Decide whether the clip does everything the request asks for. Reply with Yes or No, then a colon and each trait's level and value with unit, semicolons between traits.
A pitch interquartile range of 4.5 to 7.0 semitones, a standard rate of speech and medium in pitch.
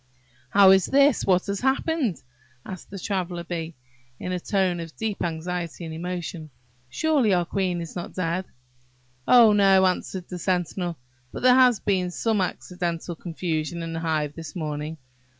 No: average, 2.9 semitones; average, 160 wpm; medium, 180 Hz